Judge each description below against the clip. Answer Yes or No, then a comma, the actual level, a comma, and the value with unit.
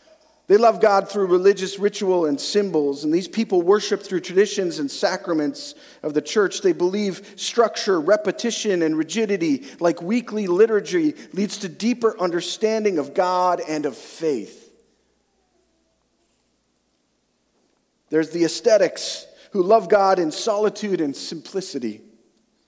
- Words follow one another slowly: Yes, slow, 125 wpm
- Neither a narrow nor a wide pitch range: Yes, average, 4.2 semitones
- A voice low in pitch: No, high, 195 Hz